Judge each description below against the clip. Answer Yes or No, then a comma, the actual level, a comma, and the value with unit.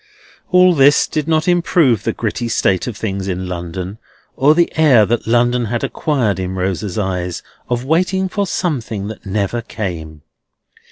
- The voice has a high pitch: No, low, 115 Hz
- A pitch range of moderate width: No, wide, 7.8 semitones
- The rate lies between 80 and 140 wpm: No, average, 160 wpm